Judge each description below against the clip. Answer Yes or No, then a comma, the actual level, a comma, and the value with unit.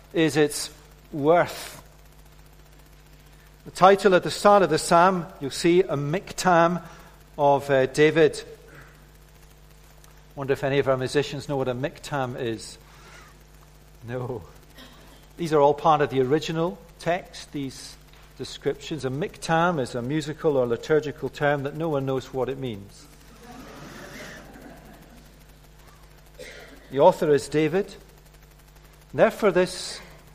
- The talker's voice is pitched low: No, medium, 150 Hz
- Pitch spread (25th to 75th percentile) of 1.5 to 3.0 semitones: No, average, 3.8 semitones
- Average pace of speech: No, slow, 125 wpm